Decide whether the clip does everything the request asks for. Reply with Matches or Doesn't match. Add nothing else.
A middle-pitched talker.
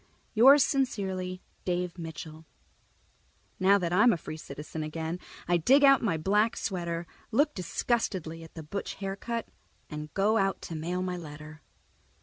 Matches